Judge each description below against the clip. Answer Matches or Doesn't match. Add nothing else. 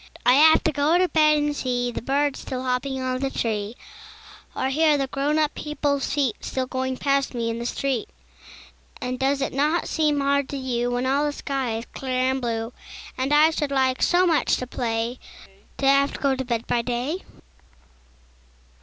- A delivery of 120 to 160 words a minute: Doesn't match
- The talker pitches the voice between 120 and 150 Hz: Doesn't match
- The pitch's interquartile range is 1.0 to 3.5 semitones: Matches